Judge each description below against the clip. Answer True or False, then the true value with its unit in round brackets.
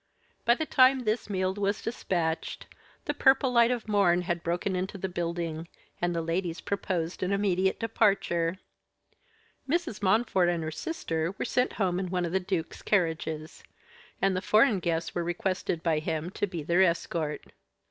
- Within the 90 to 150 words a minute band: False (170 wpm)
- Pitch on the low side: False (185 Hz)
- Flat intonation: False (3.4 semitones)